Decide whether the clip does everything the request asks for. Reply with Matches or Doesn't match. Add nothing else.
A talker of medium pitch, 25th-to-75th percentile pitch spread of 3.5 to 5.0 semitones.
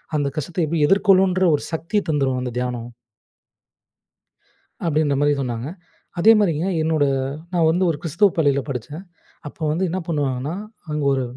Matches